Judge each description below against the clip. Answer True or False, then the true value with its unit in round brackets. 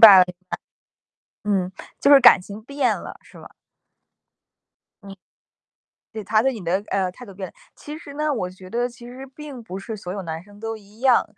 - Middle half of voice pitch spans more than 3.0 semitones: True (4.7 semitones)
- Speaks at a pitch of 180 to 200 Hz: False (215 Hz)